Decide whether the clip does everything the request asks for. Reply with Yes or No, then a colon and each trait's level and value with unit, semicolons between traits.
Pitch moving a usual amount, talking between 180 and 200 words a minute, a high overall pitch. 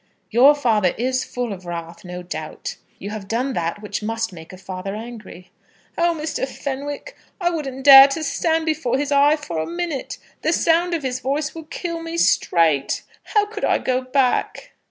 No: wide, 7.4 semitones; average, 185 wpm; very high, 260 Hz